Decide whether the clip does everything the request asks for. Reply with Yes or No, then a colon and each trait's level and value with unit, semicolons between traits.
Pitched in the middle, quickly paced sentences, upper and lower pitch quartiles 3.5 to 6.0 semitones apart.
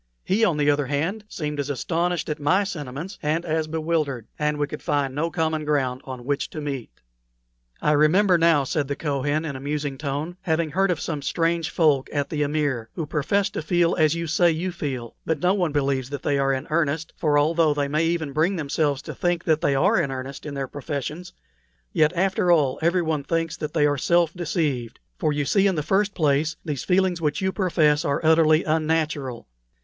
No: medium, 155 Hz; fast, 210 wpm; average, 2.8 semitones